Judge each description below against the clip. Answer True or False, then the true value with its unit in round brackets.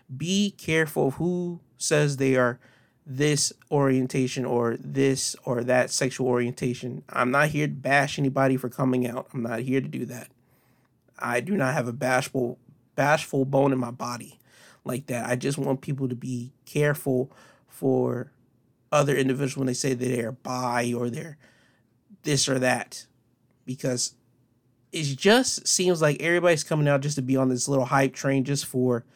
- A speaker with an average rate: True (170 wpm)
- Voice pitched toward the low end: True (130 Hz)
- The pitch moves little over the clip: True (2.2 semitones)